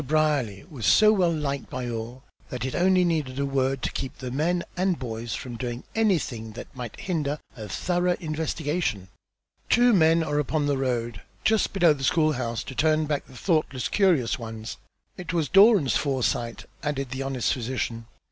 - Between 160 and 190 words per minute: Yes, average, 175 wpm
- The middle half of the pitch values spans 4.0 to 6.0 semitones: Yes, average, 5.1 semitones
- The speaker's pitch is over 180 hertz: No, medium, 140 Hz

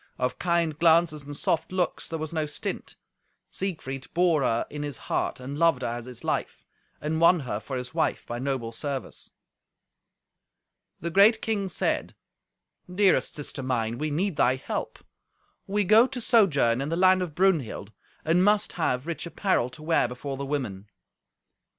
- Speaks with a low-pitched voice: No, medium, 155 Hz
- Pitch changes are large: Yes, wide, 5.7 semitones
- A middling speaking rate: Yes, average, 170 wpm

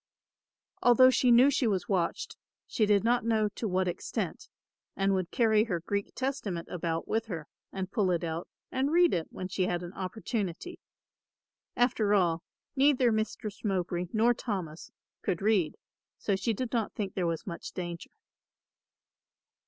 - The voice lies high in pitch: Yes, high, 200 Hz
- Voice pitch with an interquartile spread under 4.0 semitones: No, average, 4.5 semitones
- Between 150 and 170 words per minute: Yes, average, 160 wpm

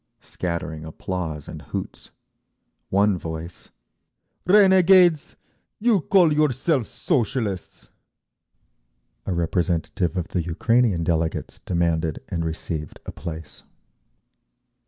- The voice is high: No, very low, 90 Hz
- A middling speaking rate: No, slow, 90 wpm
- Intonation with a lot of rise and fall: Yes, wide, 8.9 semitones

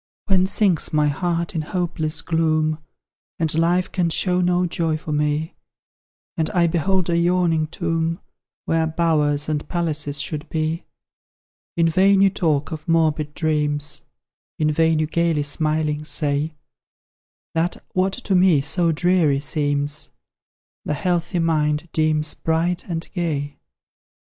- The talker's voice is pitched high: No, medium, 160 Hz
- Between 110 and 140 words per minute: Yes, slow, 135 wpm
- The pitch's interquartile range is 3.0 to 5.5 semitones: No, narrow, 2.4 semitones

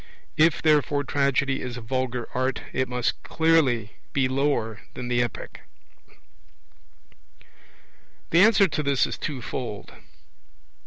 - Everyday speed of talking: No, slow, 115 wpm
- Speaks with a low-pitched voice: Yes, low, 130 Hz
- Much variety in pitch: No, average, 3.2 semitones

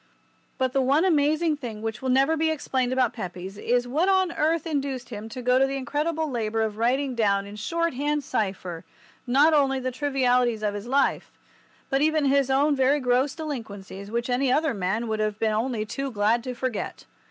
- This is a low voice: No, very high, 255 Hz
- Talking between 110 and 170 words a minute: No, average, 200 wpm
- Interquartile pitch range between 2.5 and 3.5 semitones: No, average, 4.4 semitones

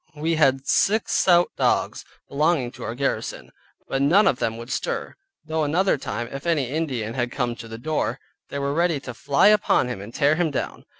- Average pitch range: Yes, average, 4.6 semitones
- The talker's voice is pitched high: No, medium, 140 Hz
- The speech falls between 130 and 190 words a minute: No, average, 200 wpm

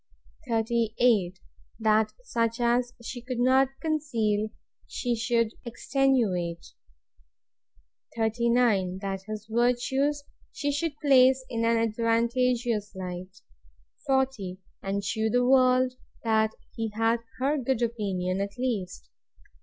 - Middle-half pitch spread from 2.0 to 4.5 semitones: Yes, average, 3.1 semitones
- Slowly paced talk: Yes, slow, 105 wpm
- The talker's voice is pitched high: Yes, high, 230 Hz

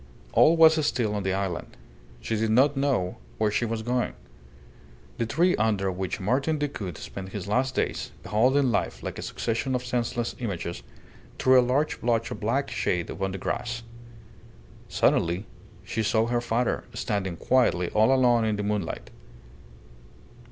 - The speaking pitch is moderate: No, low, 115 Hz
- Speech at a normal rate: Yes, average, 160 wpm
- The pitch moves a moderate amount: Yes, average, 4.1 semitones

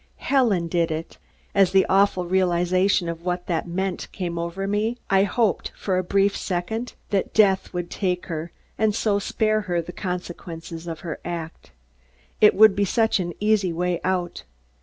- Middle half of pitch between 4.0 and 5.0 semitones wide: No, average, 2.7 semitones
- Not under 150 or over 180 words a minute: Yes, average, 170 wpm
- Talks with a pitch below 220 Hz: Yes, medium, 185 Hz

